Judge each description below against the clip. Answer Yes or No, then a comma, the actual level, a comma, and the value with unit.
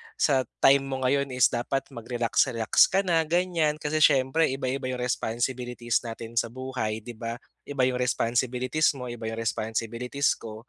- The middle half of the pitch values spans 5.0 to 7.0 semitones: No, average, 2.8 semitones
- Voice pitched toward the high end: No, low, 125 Hz